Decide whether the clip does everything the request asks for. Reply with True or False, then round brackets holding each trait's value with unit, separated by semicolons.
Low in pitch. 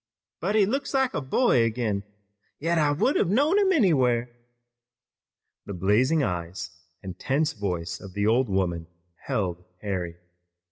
True (120 Hz)